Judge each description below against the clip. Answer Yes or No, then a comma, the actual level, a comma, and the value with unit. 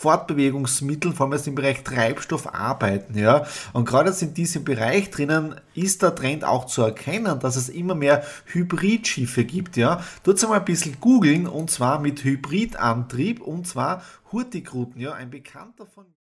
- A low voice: No, medium, 145 Hz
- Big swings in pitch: Yes, wide, 5.7 semitones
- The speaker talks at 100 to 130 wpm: No, average, 165 wpm